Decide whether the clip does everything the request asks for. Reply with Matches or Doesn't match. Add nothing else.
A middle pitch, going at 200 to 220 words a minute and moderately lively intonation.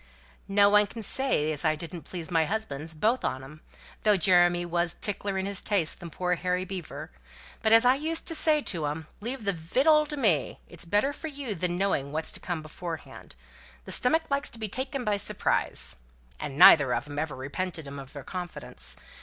Doesn't match